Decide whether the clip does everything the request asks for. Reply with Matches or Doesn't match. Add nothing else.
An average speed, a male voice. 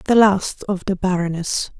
Doesn't match